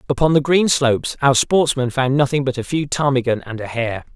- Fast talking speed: Yes, fast, 215 wpm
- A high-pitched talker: No, low, 135 Hz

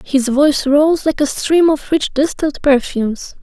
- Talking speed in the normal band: Yes, average, 175 wpm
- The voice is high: Yes, very high, 285 Hz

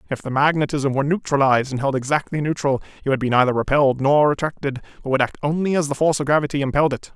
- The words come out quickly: Yes, fast, 225 wpm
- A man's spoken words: Yes, male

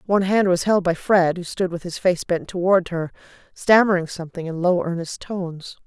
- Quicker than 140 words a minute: Yes, fast, 205 wpm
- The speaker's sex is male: No, female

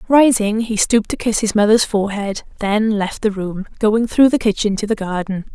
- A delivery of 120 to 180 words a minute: No, fast, 205 wpm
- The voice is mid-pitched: No, high, 210 Hz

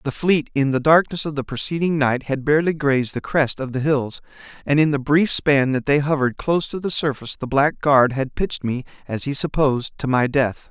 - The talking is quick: Yes, fast, 230 wpm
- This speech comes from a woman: No, male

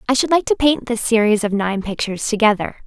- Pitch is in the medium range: No, high, 230 Hz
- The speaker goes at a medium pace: No, fast, 230 wpm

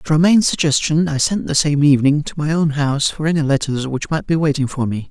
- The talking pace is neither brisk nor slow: No, fast, 245 wpm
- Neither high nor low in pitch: Yes, medium, 150 Hz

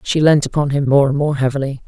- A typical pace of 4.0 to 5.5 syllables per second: No, 6.3 syllables/s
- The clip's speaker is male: No, female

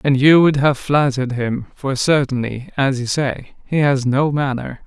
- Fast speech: No, average, 185 wpm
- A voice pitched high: No, low, 135 Hz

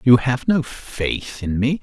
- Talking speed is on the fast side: No, average, 195 wpm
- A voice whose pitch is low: Yes, low, 125 Hz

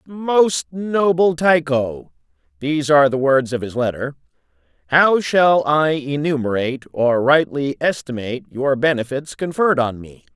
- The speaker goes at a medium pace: No, slow, 130 wpm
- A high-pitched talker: No, medium, 145 Hz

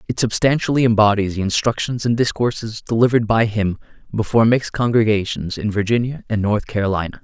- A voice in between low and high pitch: No, low, 110 Hz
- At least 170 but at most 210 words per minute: No, average, 150 wpm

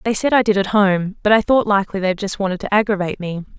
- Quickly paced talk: Yes, fast, 270 wpm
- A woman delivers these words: Yes, female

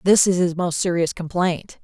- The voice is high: No, medium, 175 Hz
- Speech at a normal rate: Yes, average, 195 wpm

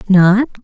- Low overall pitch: No, high, 205 Hz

